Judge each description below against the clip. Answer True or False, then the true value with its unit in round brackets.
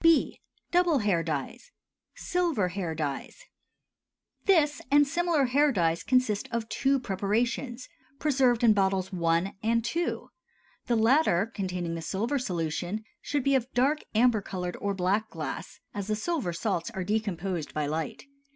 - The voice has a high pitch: True (215 Hz)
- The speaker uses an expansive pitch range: True (6.8 semitones)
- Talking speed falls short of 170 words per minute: True (145 wpm)